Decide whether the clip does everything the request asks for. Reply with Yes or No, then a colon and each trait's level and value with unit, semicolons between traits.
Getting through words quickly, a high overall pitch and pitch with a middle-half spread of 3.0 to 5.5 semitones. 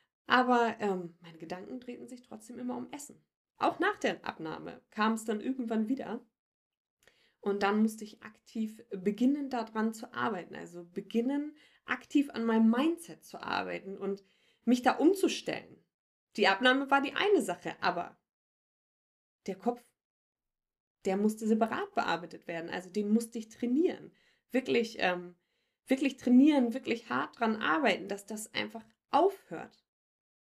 No: average, 140 wpm; high, 235 Hz; average, 3.7 semitones